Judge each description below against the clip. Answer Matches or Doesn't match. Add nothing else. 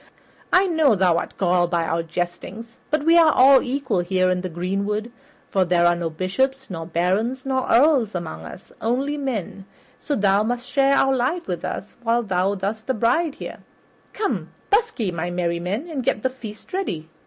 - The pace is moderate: Matches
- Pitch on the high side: Matches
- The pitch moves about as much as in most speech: Doesn't match